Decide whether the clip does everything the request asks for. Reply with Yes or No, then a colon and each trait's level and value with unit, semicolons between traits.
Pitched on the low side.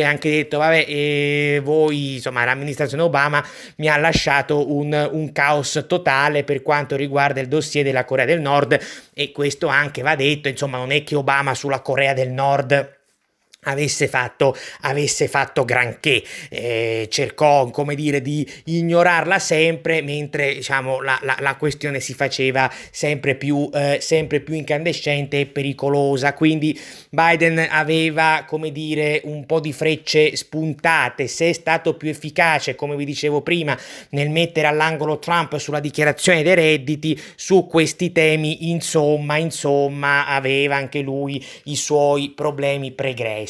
No: medium, 145 Hz